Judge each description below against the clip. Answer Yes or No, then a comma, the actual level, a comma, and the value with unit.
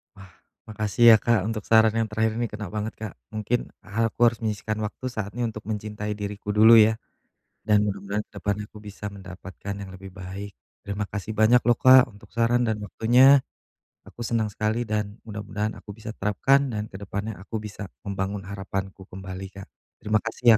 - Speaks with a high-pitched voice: No, low, 105 Hz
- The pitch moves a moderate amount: No, narrow, 1.8 semitones